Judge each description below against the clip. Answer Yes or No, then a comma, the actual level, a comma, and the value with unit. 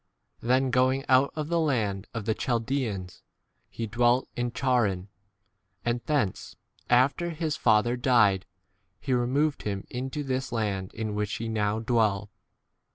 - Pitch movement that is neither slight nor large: Yes, average, 3.7 semitones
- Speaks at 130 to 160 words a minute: Yes, average, 150 wpm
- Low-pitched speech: Yes, low, 120 Hz